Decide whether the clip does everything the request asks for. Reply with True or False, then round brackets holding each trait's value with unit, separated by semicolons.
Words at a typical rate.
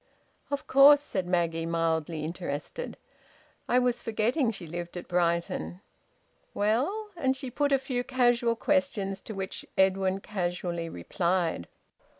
False (130 wpm)